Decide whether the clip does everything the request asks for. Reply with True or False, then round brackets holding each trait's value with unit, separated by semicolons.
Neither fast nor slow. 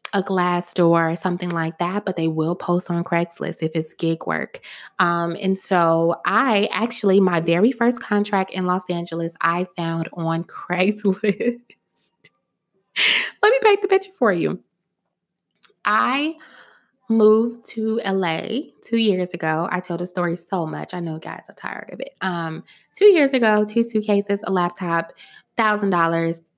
True (160 wpm)